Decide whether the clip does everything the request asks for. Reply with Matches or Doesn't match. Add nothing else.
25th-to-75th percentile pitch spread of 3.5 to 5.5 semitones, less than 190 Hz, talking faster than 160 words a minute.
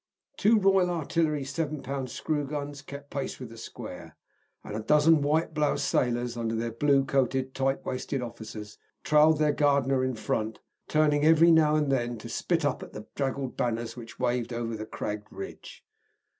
Matches